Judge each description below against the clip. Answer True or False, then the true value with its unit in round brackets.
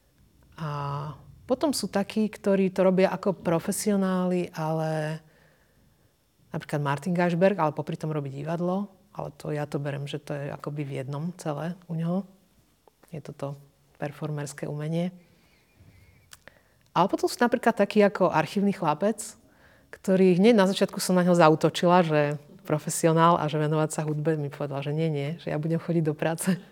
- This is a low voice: False (165 Hz)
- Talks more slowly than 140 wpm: False (155 wpm)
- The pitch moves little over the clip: False (3.8 semitones)